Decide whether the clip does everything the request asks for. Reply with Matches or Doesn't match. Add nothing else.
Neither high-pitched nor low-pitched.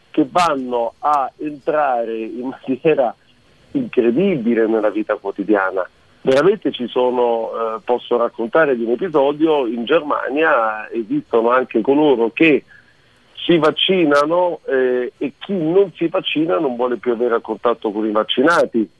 Doesn't match